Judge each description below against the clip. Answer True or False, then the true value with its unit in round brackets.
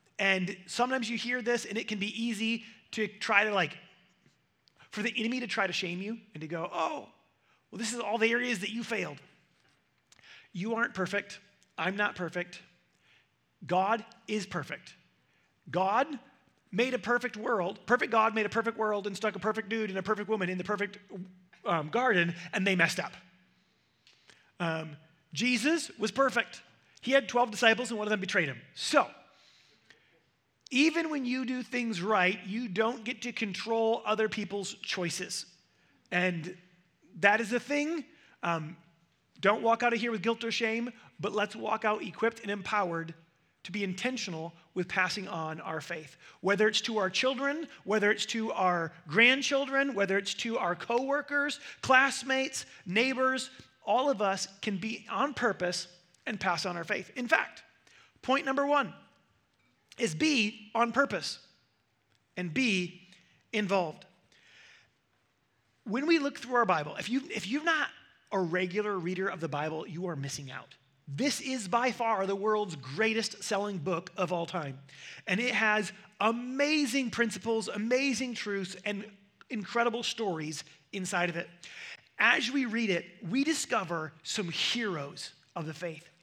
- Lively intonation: False (4.6 semitones)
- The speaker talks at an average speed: True (160 wpm)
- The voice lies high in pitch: True (210 Hz)